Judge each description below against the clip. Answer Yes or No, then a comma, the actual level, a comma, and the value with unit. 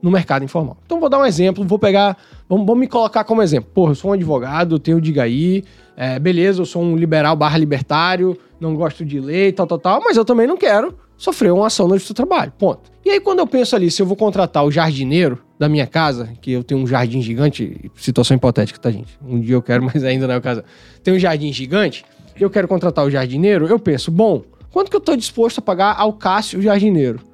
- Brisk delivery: Yes, fast, 235 wpm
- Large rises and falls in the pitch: Yes, wide, 6.6 semitones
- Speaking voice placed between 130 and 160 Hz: No, medium, 170 Hz